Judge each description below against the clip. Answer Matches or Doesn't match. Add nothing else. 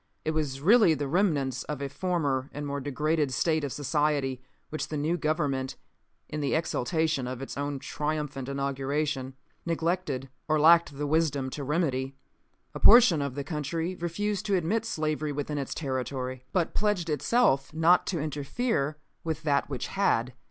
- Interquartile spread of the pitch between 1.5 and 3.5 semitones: Matches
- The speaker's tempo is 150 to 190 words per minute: Matches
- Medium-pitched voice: Matches